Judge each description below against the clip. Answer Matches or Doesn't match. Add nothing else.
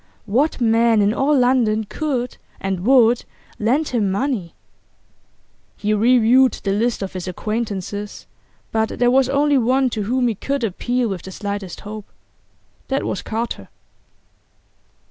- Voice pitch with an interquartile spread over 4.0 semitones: Doesn't match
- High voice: Matches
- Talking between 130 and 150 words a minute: Matches